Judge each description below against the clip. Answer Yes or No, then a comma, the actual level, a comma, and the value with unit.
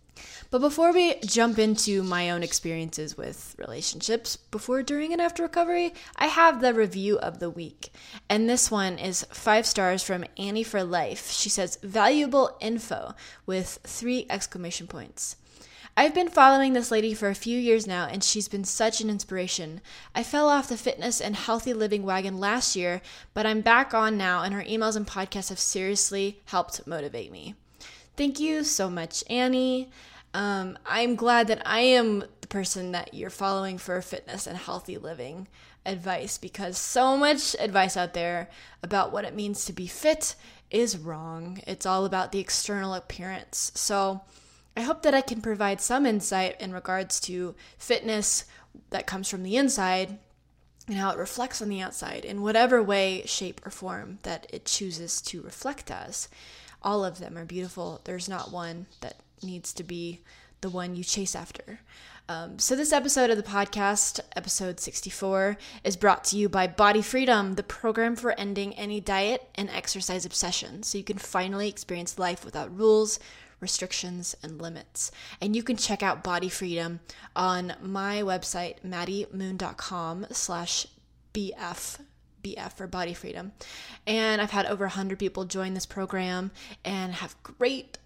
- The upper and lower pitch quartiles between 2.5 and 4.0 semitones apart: Yes, average, 3.6 semitones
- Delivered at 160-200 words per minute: Yes, average, 165 wpm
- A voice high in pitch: Yes, high, 200 Hz